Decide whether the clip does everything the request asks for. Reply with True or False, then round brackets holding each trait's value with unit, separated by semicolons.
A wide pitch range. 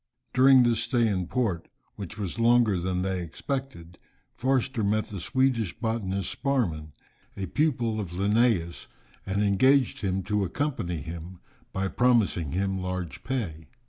False (4.9 semitones)